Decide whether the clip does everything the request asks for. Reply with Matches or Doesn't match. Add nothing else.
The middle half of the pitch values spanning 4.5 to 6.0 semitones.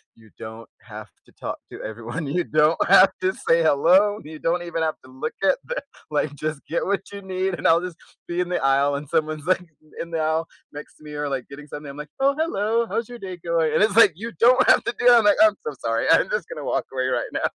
Matches